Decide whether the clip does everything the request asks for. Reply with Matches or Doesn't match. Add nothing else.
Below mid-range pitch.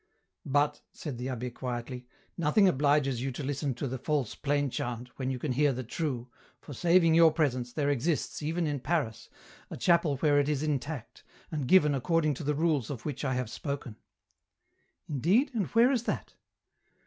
Doesn't match